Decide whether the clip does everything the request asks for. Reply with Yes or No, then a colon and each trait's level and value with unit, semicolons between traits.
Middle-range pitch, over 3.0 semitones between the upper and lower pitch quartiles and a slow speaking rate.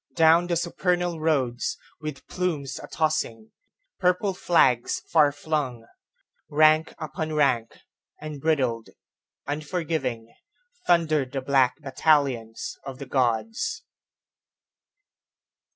Yes: medium, 150 Hz; average, 4.1 semitones; slow, 80 wpm